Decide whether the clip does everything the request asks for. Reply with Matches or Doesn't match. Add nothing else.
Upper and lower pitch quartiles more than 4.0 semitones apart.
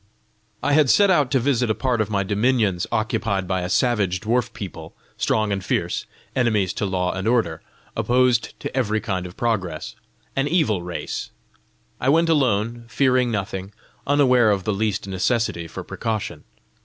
Matches